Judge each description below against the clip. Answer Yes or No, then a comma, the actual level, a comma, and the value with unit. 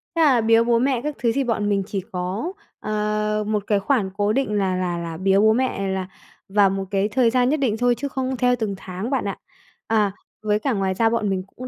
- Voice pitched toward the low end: No, high, 215 Hz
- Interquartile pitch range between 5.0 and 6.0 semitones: No, average, 3.9 semitones